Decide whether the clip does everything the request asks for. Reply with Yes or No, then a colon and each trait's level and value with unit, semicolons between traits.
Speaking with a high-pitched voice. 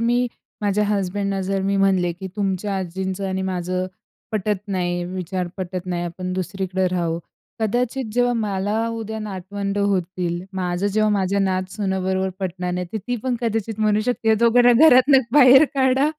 Yes: high, 195 Hz